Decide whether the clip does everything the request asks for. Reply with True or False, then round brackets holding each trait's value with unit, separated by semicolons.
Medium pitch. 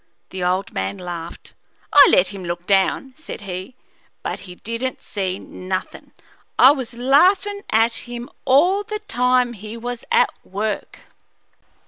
False (230 Hz)